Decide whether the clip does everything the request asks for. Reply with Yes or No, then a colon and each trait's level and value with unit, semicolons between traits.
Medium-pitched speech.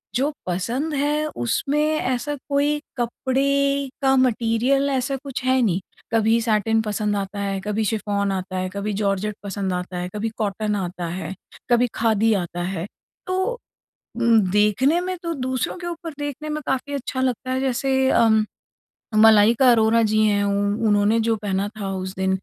No: high, 225 Hz